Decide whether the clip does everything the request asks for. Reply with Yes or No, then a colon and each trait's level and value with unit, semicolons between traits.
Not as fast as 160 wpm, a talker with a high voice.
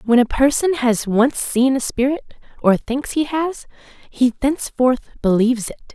Yes: average, 140 wpm; very high, 260 Hz